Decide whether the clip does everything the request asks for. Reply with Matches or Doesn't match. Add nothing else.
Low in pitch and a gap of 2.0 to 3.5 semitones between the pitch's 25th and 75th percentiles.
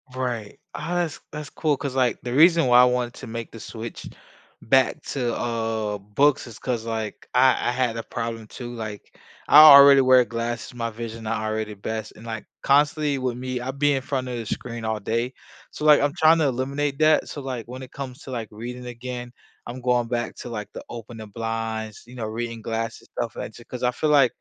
Matches